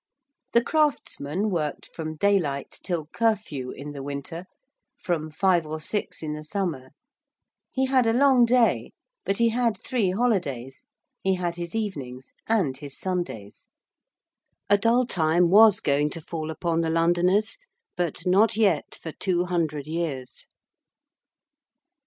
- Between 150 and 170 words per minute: No, average, 140 wpm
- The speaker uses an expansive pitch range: Yes, wide, 5.8 semitones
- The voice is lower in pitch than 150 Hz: No, medium, 175 Hz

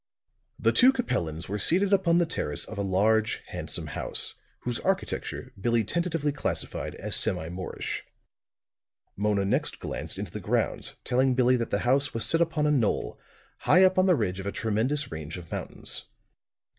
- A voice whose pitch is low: Yes, low, 120 Hz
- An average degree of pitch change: No, wide, 8.7 semitones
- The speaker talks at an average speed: Yes, average, 170 wpm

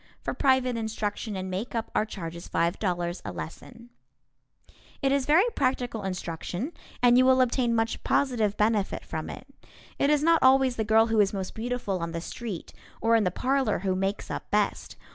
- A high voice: Yes, high, 225 Hz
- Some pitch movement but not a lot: Yes, average, 4.8 semitones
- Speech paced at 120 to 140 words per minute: No, average, 180 wpm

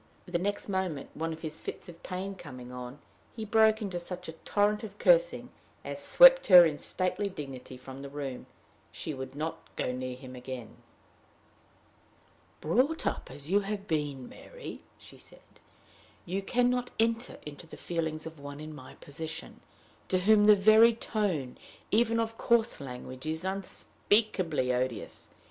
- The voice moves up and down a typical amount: No, wide, 6.9 semitones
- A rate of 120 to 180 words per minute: Yes, average, 160 wpm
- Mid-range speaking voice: Yes, medium, 170 Hz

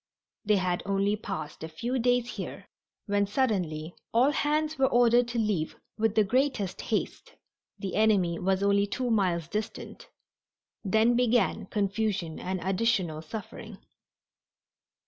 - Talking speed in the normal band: No, slow, 130 wpm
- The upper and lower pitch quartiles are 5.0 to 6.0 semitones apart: No, average, 4.1 semitones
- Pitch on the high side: Yes, high, 205 Hz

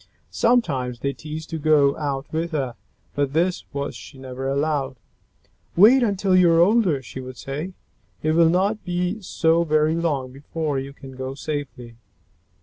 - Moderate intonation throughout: Yes, average, 4.2 semitones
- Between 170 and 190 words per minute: No, average, 155 wpm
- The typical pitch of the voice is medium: Yes, medium, 155 Hz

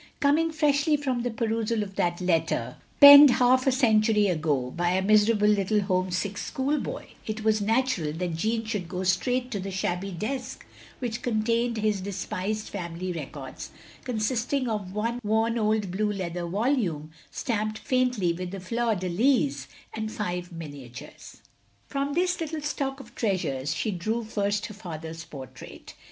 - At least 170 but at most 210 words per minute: No, average, 155 wpm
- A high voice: Yes, high, 210 Hz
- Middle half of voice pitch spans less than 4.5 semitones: No, average, 4.9 semitones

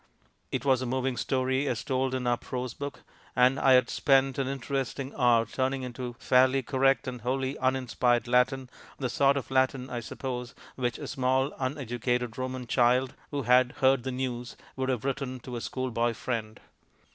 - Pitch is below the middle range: Yes, low, 130 Hz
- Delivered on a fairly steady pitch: Yes, narrow, 1.4 semitones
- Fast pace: No, average, 180 wpm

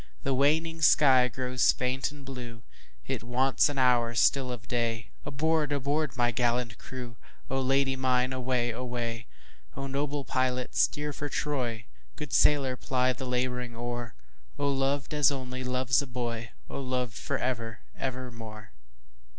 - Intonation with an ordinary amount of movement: No, narrow, 2.3 semitones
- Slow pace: Yes, slow, 125 wpm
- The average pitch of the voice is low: Yes, low, 125 Hz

